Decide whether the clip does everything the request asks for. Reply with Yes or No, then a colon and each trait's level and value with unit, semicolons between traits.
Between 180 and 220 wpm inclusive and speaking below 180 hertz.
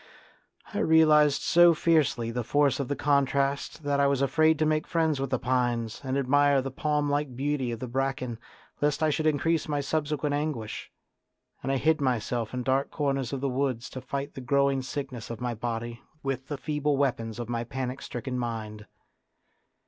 Yes: average, 185 wpm; low, 135 Hz